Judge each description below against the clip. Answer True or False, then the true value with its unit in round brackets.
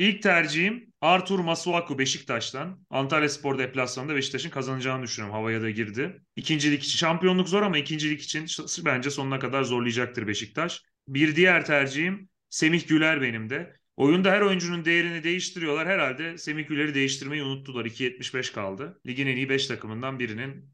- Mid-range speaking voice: True (145 Hz)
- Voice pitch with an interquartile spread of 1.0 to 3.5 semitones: False (4.4 semitones)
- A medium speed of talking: False (150 wpm)